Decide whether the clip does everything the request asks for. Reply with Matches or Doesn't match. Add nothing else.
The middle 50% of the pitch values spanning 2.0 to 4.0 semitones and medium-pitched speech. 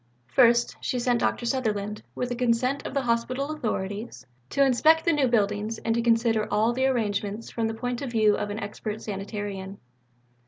Doesn't match